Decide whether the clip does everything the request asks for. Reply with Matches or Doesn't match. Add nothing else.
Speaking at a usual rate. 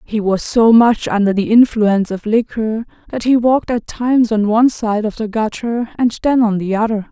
Doesn't match